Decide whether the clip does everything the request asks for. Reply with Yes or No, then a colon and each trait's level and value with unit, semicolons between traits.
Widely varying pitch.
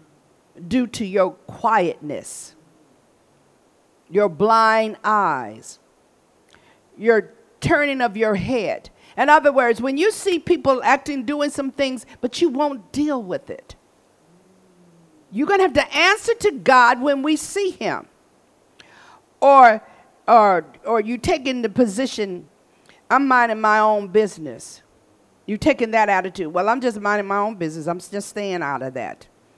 Yes: wide, 5.8 semitones